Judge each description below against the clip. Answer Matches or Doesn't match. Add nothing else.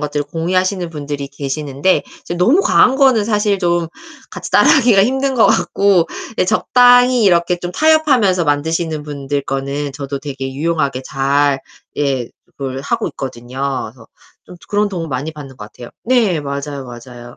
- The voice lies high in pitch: Doesn't match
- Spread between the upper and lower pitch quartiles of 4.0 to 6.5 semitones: Matches